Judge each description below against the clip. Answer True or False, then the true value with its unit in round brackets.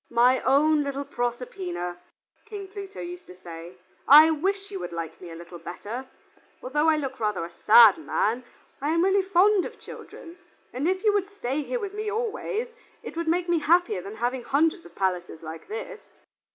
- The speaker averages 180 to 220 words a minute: True (190 wpm)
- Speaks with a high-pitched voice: True (295 Hz)